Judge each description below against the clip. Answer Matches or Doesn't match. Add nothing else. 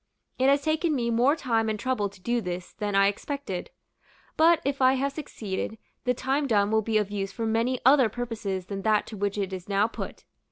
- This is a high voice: Matches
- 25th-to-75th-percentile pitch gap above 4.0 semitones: Matches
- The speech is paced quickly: Matches